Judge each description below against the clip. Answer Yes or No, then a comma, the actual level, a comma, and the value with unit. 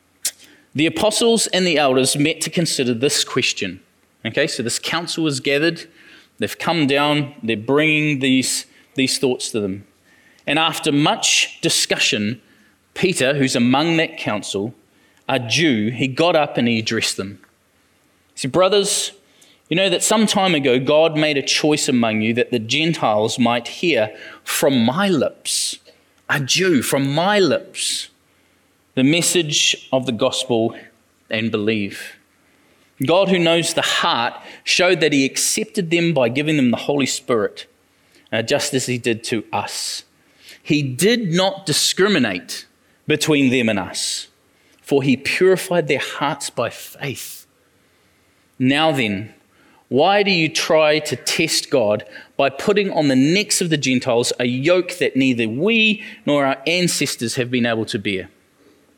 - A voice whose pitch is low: No, medium, 145 Hz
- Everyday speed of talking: Yes, average, 150 wpm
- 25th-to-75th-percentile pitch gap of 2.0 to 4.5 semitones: No, average, 5.2 semitones